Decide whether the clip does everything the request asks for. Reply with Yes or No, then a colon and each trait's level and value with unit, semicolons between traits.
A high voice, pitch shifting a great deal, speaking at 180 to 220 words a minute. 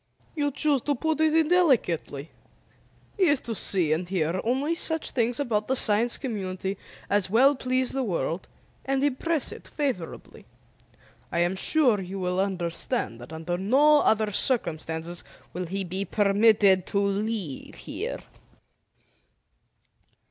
No: high, 210 Hz; wide, 6.7 semitones; slow, 135 wpm